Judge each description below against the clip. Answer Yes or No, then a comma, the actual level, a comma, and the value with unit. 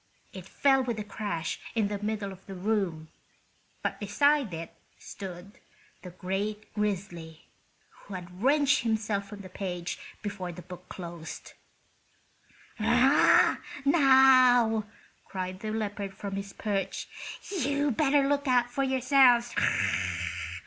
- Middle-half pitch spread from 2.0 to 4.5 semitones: No, average, 5.3 semitones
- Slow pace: Yes, slow, 120 wpm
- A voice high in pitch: Yes, high, 210 Hz